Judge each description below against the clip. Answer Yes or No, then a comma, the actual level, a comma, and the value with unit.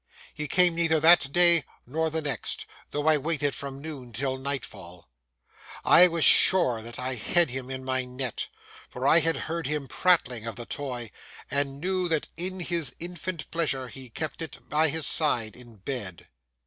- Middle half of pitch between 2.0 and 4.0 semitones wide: No, average, 4.4 semitones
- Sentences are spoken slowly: No, average, 175 wpm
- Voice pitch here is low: No, medium, 145 Hz